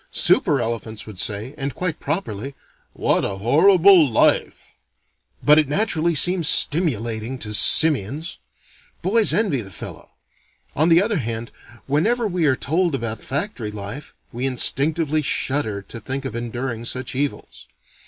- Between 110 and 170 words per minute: Yes, average, 140 wpm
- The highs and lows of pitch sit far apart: Yes, wide, 6.2 semitones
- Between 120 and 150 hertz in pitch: Yes, low, 135 Hz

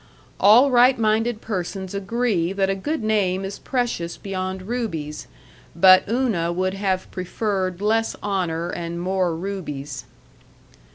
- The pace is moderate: No, slow, 125 wpm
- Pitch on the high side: Yes, high, 195 Hz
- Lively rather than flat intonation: No, average, 3.4 semitones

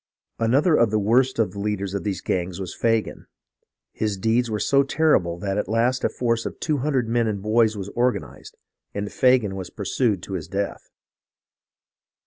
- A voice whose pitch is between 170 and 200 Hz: No, low, 110 Hz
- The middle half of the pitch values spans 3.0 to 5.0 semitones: Yes, average, 3.6 semitones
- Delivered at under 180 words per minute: No, average, 185 wpm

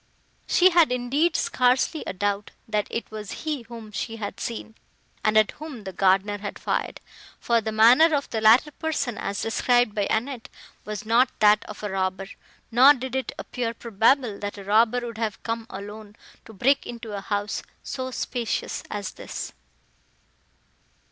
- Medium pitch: No, high, 225 Hz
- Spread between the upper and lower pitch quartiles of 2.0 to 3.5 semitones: Yes, average, 3.2 semitones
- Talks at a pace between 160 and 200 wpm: Yes, average, 170 wpm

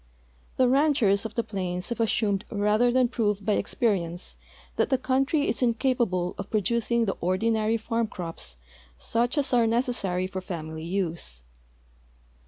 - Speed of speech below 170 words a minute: Yes, average, 150 wpm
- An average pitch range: Yes, average, 4.4 semitones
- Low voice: No, high, 215 Hz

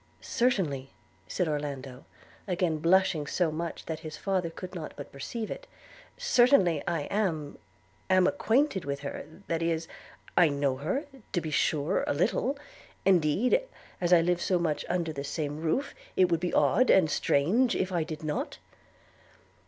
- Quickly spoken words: No, average, 170 wpm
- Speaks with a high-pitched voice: No, medium, 165 Hz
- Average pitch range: Yes, average, 4.2 semitones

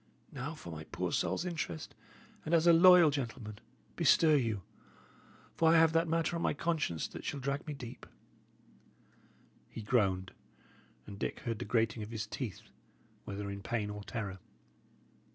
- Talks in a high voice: No, low, 120 Hz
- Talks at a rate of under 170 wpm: Yes, average, 160 wpm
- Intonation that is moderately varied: No, wide, 7.7 semitones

